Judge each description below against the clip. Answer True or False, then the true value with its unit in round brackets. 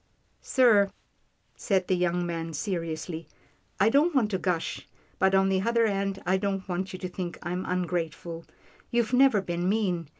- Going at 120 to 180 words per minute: True (175 wpm)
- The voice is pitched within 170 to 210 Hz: True (190 Hz)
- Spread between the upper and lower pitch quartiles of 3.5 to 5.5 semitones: False (2.7 semitones)